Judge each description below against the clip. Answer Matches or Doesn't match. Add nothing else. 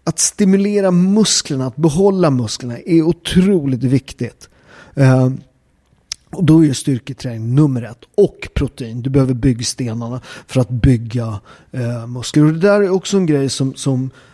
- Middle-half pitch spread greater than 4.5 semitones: Matches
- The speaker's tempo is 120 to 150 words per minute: Matches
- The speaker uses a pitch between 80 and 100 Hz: Doesn't match